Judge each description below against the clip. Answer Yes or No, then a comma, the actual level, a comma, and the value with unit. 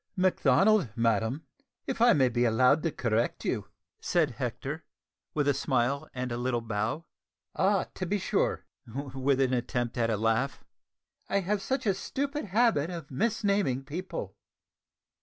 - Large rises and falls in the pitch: Yes, wide, 7.5 semitones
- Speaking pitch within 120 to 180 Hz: Yes, medium, 140 Hz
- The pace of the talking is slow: No, average, 150 wpm